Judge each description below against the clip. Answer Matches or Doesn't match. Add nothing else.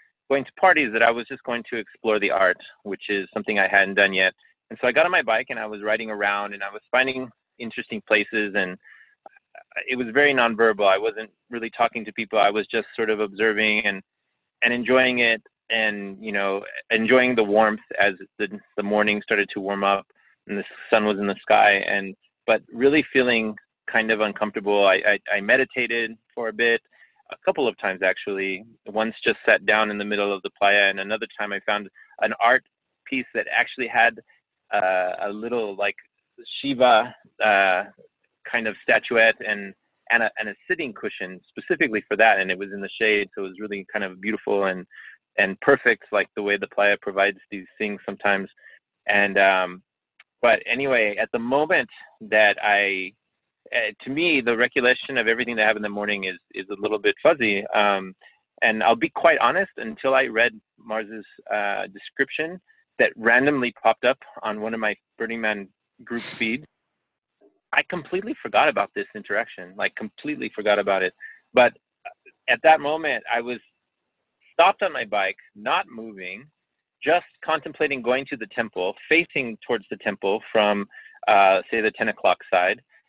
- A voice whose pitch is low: Matches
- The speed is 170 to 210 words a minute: Matches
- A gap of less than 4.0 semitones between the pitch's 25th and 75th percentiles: Matches